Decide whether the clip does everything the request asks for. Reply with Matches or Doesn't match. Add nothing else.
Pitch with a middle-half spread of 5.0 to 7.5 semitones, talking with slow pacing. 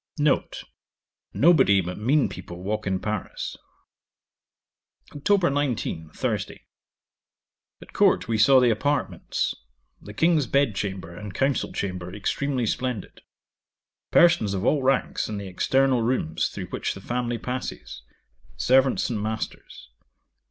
Matches